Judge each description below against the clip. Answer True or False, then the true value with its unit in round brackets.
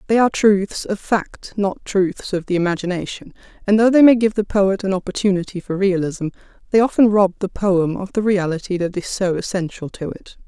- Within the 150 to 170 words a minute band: False (200 wpm)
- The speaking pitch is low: False (195 Hz)